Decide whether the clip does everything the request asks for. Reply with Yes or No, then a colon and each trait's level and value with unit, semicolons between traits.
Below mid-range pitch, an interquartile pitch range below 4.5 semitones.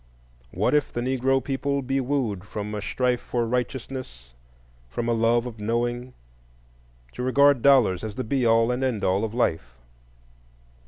Yes: low, 120 Hz; average, 3.2 semitones